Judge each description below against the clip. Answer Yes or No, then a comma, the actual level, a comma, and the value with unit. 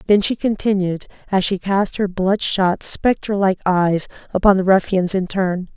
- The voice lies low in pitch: No, high, 190 Hz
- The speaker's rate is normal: Yes, average, 175 wpm